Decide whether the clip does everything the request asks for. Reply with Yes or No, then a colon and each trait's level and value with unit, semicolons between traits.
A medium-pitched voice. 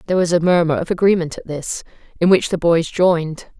Yes: medium, 170 Hz